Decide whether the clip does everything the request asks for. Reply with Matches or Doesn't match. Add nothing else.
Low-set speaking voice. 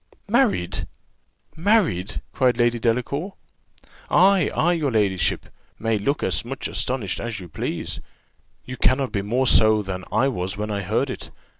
Matches